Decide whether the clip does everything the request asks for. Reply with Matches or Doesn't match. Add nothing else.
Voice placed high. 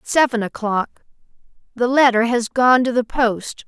Matches